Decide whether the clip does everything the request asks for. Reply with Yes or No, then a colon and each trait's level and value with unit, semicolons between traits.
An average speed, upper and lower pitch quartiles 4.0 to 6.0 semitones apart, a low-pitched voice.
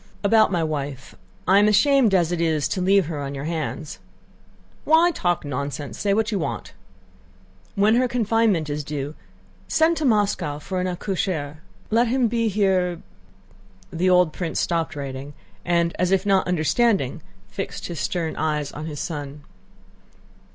No: average, 160 wpm; wide, 5.5 semitones; medium, 175 Hz